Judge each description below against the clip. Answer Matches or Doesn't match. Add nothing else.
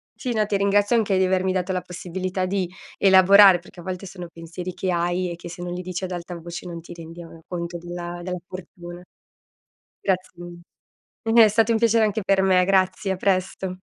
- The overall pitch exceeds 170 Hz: Matches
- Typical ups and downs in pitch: Doesn't match